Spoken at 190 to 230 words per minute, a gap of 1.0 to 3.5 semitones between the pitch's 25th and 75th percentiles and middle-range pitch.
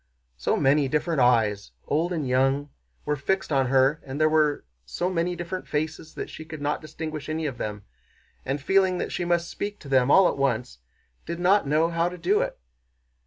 No: average, 200 wpm; average, 4.2 semitones; medium, 155 Hz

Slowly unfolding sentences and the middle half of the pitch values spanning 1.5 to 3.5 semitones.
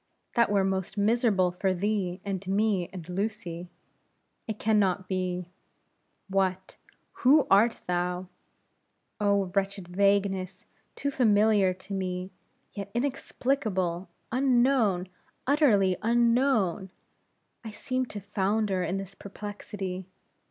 Yes: slow, 110 wpm; average, 2.9 semitones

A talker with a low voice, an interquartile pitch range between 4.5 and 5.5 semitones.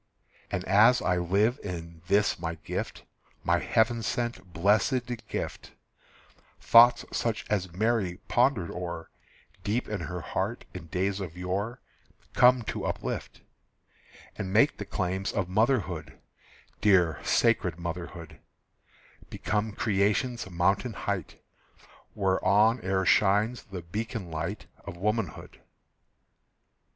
No: low, 100 Hz; average, 4.0 semitones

